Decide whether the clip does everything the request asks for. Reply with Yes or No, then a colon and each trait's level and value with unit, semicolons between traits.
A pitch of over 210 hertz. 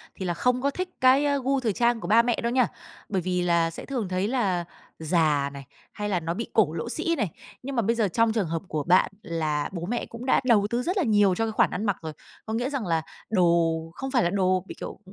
No: high, 205 Hz